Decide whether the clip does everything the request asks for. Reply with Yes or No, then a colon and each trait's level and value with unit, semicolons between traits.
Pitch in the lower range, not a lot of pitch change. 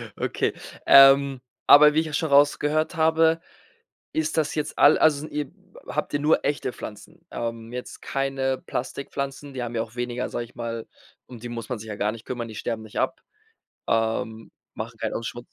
No: low, 130 Hz; average, 4.2 semitones